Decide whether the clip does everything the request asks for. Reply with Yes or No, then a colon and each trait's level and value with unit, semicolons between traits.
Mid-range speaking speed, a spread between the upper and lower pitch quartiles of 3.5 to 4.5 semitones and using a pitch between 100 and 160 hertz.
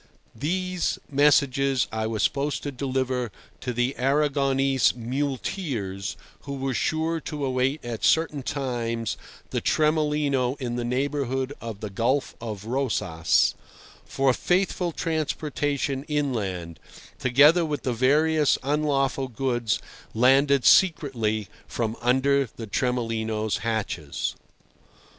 No: slow, 110 wpm; average, 3.8 semitones; low, 135 Hz